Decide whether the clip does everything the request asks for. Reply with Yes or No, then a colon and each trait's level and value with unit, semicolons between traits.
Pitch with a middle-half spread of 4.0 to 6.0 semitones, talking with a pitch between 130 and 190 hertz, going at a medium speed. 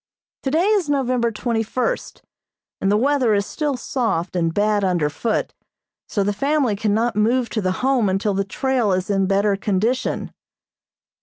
No: average, 4.6 semitones; high, 220 Hz; average, 160 wpm